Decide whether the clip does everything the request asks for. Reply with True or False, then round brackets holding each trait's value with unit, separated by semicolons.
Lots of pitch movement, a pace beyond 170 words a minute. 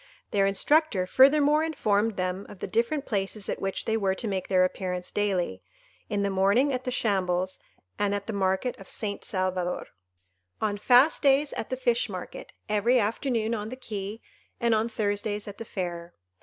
False (3.6 semitones; 180 wpm)